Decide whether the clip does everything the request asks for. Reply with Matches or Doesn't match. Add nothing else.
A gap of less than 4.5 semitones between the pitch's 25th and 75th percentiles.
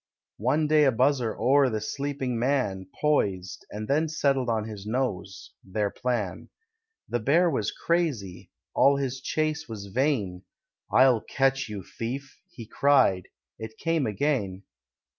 Doesn't match